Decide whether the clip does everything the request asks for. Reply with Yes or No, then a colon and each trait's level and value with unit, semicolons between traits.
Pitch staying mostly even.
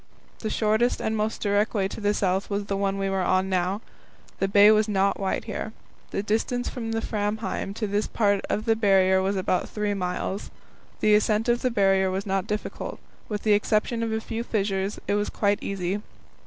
Yes: narrow, 1.9 semitones